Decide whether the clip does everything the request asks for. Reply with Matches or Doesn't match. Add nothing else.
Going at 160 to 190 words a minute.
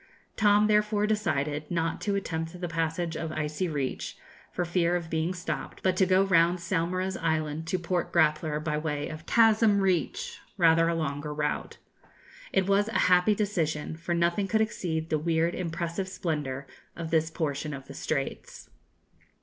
Matches